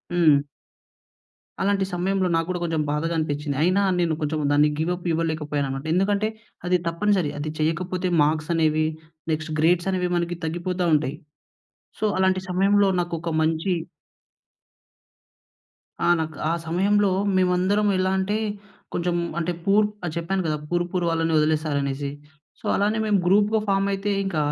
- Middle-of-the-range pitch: Yes, medium, 175 Hz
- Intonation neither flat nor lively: Yes, average, 3.3 semitones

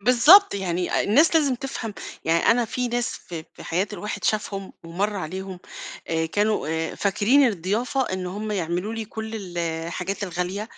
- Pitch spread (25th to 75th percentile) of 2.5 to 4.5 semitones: Yes, average, 4.0 semitones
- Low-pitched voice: No, high, 200 Hz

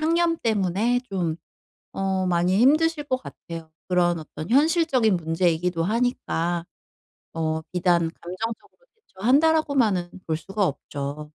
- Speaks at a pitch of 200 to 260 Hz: No, medium, 185 Hz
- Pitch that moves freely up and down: Yes, wide, 6.9 semitones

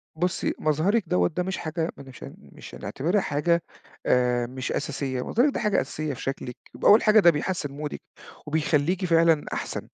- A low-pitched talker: No, medium, 155 Hz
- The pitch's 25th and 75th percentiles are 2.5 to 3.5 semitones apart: No, average, 4.7 semitones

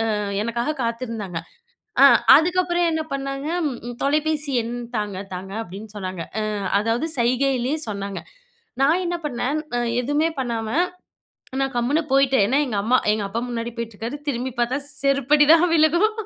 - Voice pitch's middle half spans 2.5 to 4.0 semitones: No, average, 4.5 semitones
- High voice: Yes, very high, 255 Hz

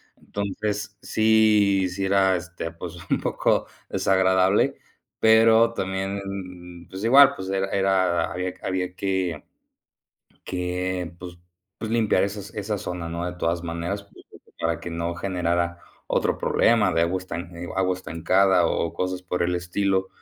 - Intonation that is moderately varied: No, narrow, 2.2 semitones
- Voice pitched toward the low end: Yes, very low, 95 Hz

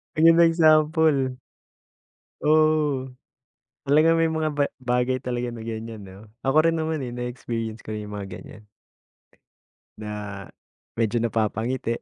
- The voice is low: Yes, low, 125 Hz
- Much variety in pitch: Yes, wide, 5.8 semitones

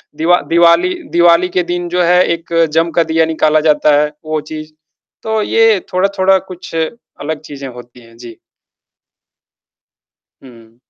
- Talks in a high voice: No, medium, 165 Hz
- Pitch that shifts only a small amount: No, average, 3.1 semitones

